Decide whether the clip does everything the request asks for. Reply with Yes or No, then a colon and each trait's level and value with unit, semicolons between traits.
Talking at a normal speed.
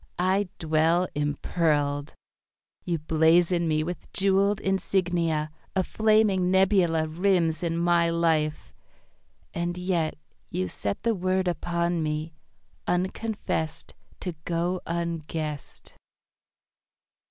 No: slow, 95 wpm